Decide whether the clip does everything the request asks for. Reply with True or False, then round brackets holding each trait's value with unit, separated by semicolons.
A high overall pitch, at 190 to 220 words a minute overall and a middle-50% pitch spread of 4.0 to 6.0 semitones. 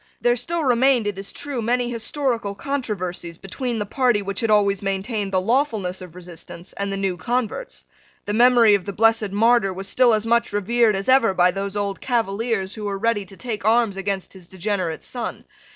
False (210 Hz; 195 wpm; 3.5 semitones)